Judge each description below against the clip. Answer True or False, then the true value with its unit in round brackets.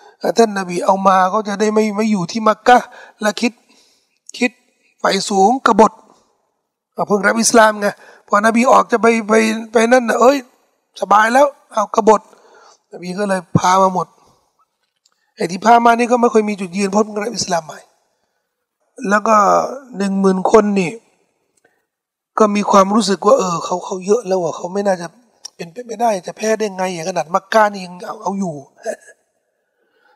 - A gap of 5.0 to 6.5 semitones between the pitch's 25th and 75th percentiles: False (3.5 semitones)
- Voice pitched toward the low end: False (215 Hz)